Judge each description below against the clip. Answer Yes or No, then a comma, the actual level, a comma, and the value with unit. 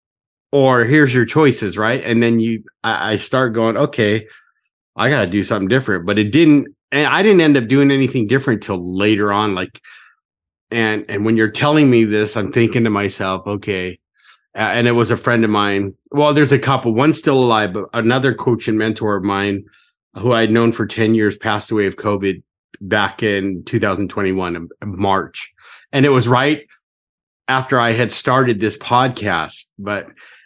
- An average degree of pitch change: Yes, average, 3.9 semitones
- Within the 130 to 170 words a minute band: No, average, 185 wpm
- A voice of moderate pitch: No, low, 115 Hz